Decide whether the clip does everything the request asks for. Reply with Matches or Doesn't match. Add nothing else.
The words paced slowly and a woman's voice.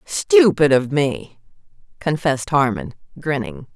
Matches